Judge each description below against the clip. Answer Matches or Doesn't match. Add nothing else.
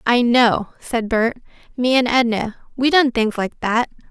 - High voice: Matches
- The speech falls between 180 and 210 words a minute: Doesn't match